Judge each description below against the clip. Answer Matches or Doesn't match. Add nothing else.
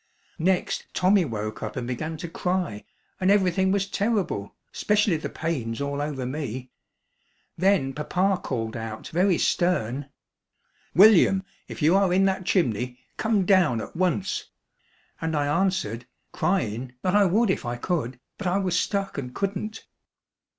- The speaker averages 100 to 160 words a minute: Matches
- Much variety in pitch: Matches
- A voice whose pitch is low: Doesn't match